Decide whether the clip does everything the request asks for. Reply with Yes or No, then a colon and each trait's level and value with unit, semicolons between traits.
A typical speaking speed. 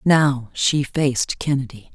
No: slow, 125 wpm